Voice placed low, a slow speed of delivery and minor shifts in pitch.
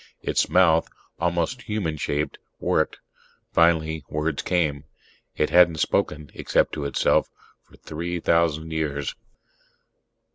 Yes: very low, 80 Hz; slow, 110 wpm; narrow, 2.0 semitones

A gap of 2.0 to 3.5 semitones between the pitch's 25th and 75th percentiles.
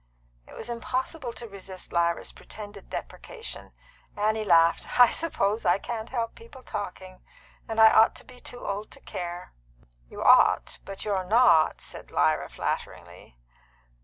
No: average, 4.3 semitones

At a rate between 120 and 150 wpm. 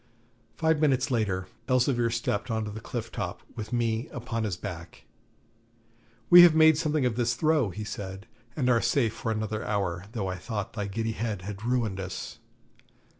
No: average, 175 wpm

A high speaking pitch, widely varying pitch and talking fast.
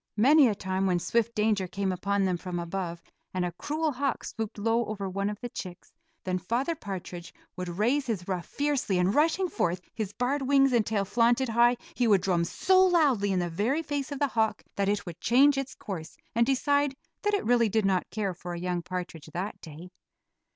Yes: high, 210 Hz; wide, 6.2 semitones; fast, 210 wpm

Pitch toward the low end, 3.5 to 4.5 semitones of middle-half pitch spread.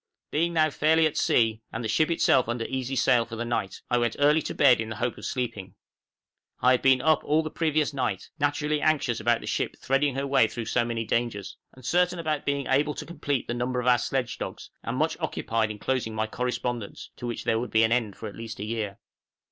Yes: low, 125 Hz; average, 4.0 semitones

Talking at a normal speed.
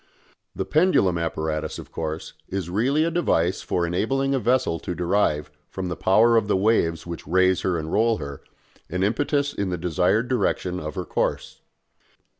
Yes: average, 175 wpm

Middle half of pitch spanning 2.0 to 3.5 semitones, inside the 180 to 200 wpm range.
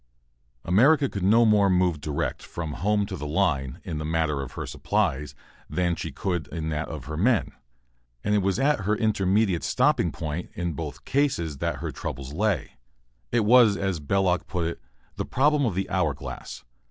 No: average, 5.3 semitones; average, 185 wpm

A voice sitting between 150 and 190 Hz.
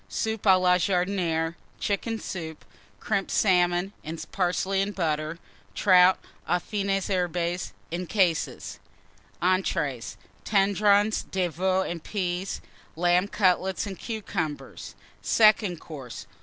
Yes: medium, 185 Hz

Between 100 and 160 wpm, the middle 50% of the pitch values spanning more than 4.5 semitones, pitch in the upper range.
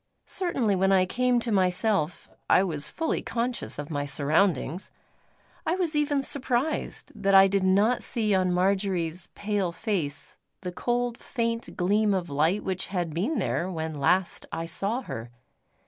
Yes: average, 155 wpm; average, 5.0 semitones; high, 195 Hz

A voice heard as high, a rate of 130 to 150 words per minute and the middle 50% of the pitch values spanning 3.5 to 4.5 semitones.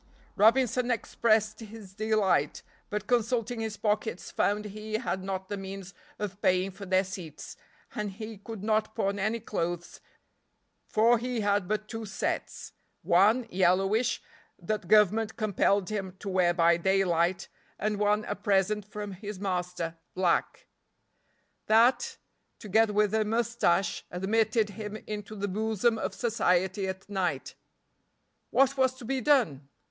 No: high, 210 Hz; average, 140 wpm; narrow, 2.6 semitones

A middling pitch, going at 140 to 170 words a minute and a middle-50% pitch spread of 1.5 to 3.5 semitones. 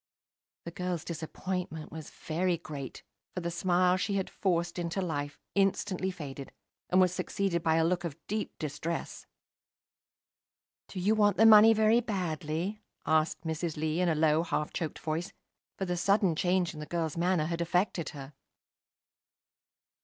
Yes: medium, 175 Hz; average, 155 wpm; average, 2.9 semitones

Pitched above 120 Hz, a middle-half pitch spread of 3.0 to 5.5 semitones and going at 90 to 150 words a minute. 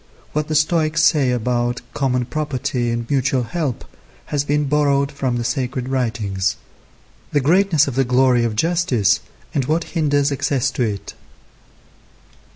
Yes: low, 135 Hz; average, 3.5 semitones; average, 145 wpm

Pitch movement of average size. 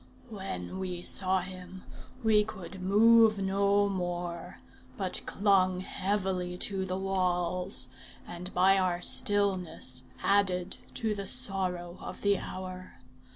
No: narrow, 1.7 semitones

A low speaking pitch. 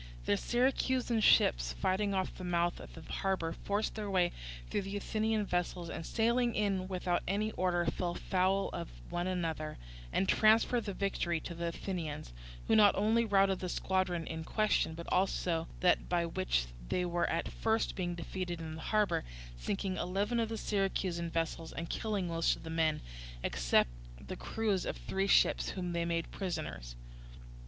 No: medium, 185 Hz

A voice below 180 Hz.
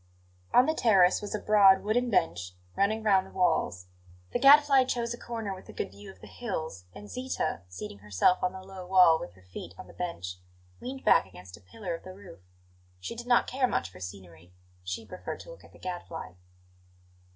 No: medium, 185 Hz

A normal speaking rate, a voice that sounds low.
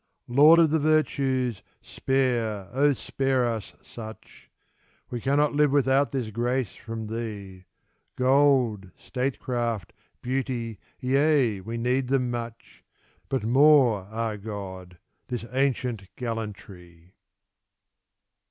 No: slow, 110 wpm; low, 120 Hz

